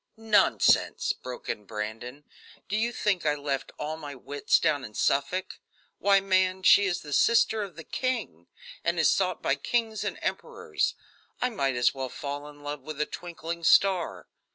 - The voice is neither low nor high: Yes, medium, 155 Hz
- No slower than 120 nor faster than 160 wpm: No, average, 175 wpm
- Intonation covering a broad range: Yes, wide, 5.9 semitones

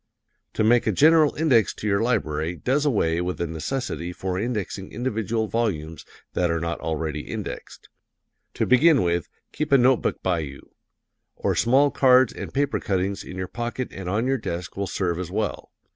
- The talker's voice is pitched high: No, low, 105 Hz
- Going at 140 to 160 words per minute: No, average, 180 wpm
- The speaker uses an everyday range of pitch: No, wide, 6.5 semitones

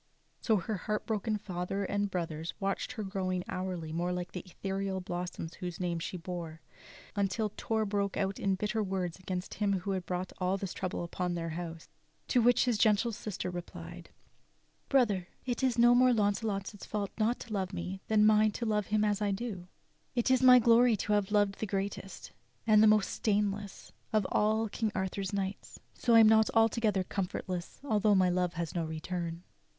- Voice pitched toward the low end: No, high, 195 Hz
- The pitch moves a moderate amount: Yes, average, 3.0 semitones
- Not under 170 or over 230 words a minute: Yes, average, 190 wpm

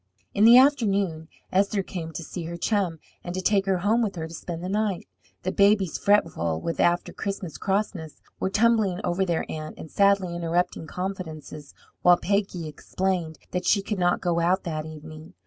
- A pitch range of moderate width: Yes, average, 3.3 semitones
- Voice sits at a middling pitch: Yes, medium, 180 Hz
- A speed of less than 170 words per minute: No, average, 180 wpm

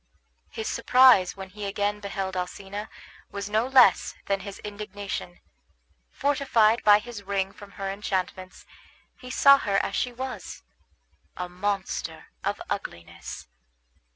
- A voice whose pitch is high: Yes, high, 200 Hz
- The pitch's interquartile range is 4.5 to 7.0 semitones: No, narrow, 2.4 semitones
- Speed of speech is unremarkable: No, slow, 125 wpm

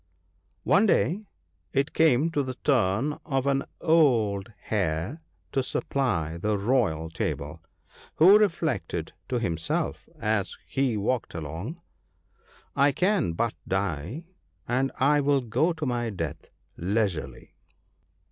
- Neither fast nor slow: No, slow, 120 wpm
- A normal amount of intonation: No, wide, 7.0 semitones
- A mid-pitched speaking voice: No, low, 120 Hz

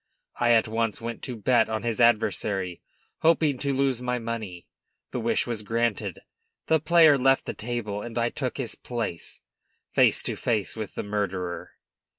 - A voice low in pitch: Yes, low, 115 Hz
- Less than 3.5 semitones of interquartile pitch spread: Yes, average, 2.8 semitones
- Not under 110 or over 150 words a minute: No, average, 165 wpm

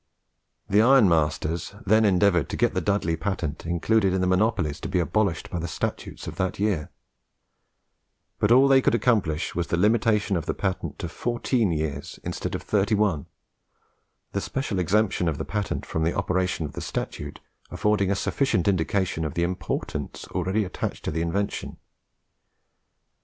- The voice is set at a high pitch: No, very low, 95 Hz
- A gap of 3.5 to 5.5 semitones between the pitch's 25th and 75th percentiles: Yes, average, 4.1 semitones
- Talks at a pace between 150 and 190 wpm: Yes, average, 165 wpm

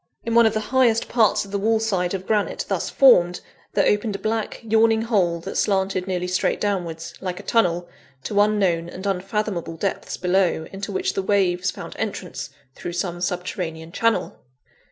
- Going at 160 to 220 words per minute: Yes, average, 175 wpm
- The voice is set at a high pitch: Yes, high, 195 Hz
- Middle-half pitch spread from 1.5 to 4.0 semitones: Yes, average, 3.4 semitones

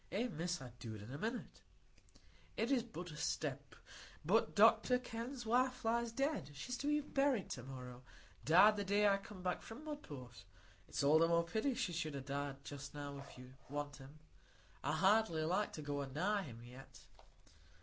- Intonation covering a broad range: Yes, wide, 8.4 semitones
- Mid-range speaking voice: Yes, medium, 170 Hz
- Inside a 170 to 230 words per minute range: Yes, average, 180 wpm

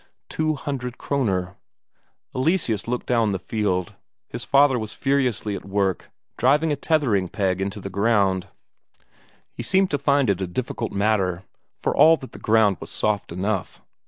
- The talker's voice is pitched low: Yes, low, 110 Hz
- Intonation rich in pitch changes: Yes, wide, 5.9 semitones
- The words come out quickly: No, average, 160 wpm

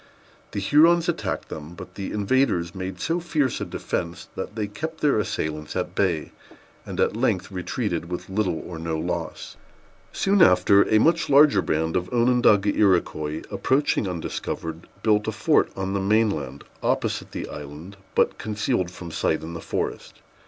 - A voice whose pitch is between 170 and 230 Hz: No, very low, 95 Hz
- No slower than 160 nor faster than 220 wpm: Yes, average, 165 wpm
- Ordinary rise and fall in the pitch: No, wide, 5.7 semitones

